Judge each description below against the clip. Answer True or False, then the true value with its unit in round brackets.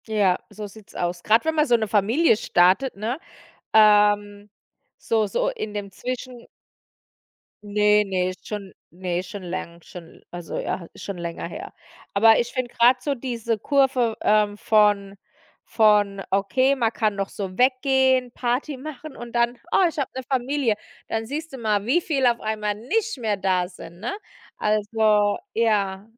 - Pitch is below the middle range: False (215 Hz)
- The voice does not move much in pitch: False (4.2 semitones)